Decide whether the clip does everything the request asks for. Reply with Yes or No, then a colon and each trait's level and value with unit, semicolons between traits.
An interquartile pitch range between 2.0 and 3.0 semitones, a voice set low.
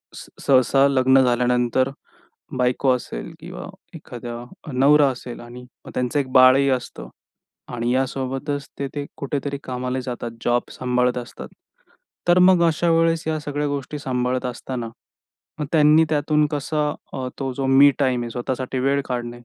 Yes: narrow, 2.4 semitones; low, 130 Hz